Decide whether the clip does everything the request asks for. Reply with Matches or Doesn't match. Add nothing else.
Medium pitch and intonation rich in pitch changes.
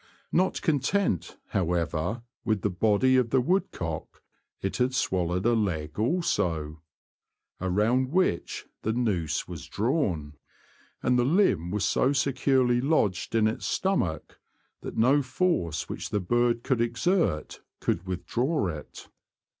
Doesn't match